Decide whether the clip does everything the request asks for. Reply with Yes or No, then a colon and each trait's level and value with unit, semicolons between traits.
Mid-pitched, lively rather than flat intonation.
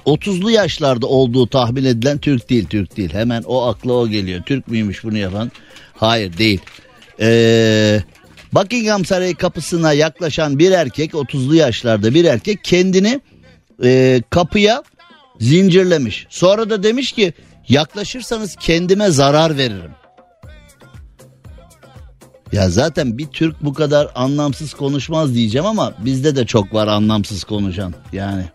No: low, 130 Hz; wide, 7.1 semitones